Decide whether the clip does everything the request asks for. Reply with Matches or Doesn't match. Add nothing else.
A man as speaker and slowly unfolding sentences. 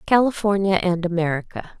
Doesn't match